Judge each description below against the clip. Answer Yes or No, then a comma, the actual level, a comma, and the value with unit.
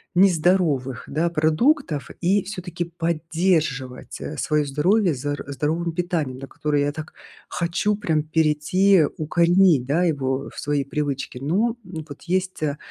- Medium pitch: Yes, medium, 160 Hz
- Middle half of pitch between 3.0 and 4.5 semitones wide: Yes, average, 3.6 semitones